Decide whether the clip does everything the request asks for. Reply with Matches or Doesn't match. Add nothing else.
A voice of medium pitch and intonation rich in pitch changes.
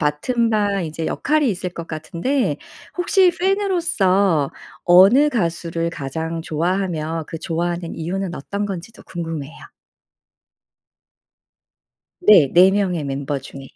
Doesn't match